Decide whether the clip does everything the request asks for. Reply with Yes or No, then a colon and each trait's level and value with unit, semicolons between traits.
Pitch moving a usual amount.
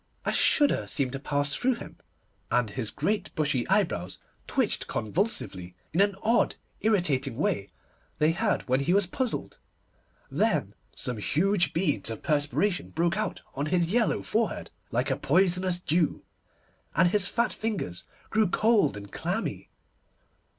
No: wide, 7.0 semitones